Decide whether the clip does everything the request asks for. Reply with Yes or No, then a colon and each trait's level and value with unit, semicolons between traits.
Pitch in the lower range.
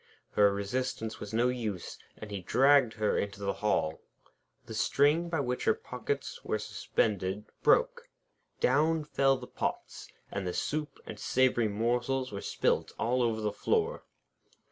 Yes: low, 120 Hz